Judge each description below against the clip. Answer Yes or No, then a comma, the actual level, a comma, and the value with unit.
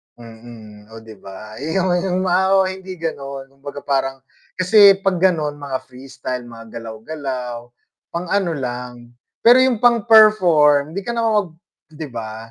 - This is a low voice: No, medium, 145 Hz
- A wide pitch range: Yes, wide, 7.7 semitones